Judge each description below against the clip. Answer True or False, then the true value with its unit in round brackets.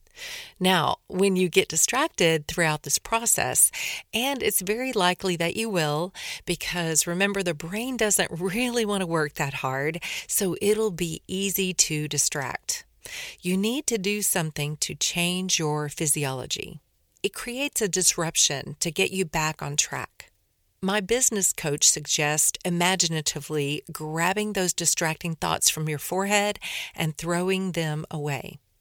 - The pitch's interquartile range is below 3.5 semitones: False (4.5 semitones)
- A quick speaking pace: False (140 wpm)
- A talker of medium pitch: True (180 Hz)